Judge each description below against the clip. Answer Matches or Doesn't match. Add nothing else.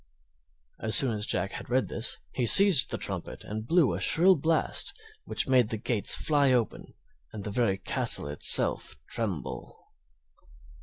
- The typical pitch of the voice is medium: Doesn't match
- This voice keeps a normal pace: Matches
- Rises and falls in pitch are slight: Doesn't match